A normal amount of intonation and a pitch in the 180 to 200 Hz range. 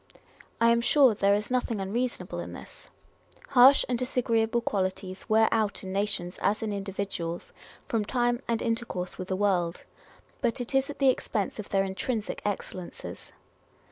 No: average, 3.7 semitones; high, 215 Hz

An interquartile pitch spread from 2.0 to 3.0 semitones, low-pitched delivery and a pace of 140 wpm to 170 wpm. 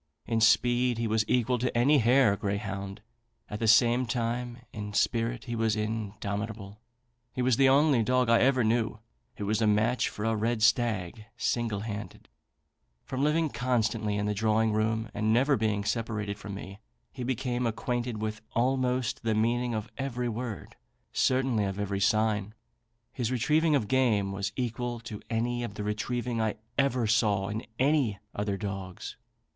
Yes: average, 2.7 semitones; low, 115 Hz; average, 165 wpm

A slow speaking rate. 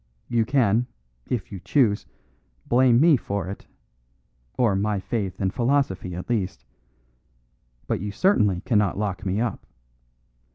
Yes: slow, 130 wpm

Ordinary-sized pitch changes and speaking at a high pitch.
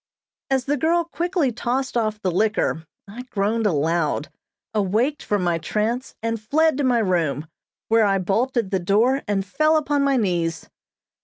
No: wide, 5.7 semitones; high, 220 Hz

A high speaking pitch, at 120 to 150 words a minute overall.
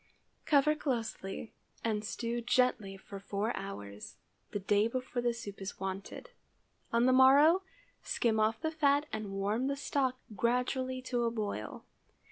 Yes: high, 235 Hz; average, 145 wpm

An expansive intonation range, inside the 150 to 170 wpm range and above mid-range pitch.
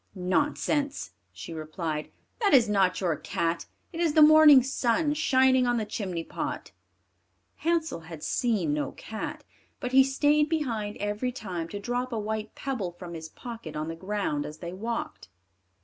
Yes: wide, 7.3 semitones; average, 165 wpm; high, 220 Hz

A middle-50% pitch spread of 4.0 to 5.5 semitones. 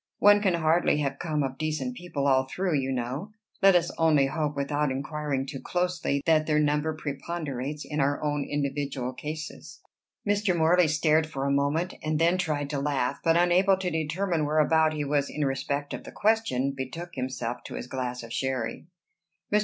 No: average, 3.3 semitones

